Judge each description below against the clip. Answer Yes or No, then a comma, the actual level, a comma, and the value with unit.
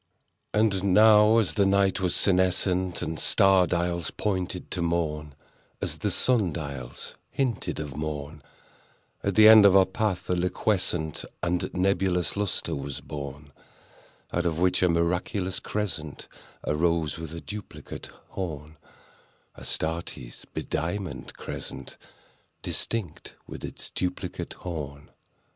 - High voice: No, very low, 90 Hz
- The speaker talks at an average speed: No, slow, 120 wpm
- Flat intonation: No, average, 3.7 semitones